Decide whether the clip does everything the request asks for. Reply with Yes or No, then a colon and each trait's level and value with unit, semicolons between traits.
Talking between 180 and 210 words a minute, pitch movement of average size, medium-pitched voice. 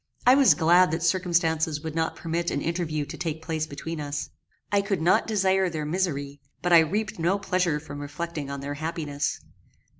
Yes: average, 185 wpm; average, 3.2 semitones; medium, 165 Hz